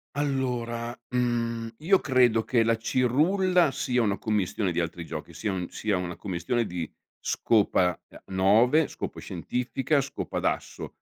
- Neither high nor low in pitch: No, low, 115 Hz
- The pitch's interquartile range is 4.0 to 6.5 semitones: Yes, average, 5.2 semitones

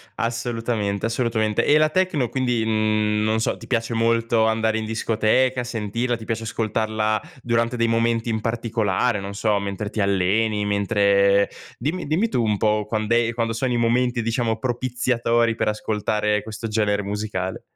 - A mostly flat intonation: Yes, narrow, 1.8 semitones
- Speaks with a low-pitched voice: Yes, low, 115 Hz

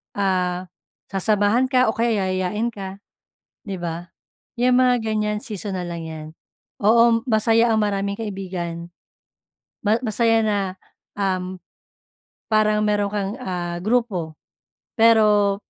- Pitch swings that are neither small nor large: Yes, average, 3.2 semitones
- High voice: Yes, high, 205 Hz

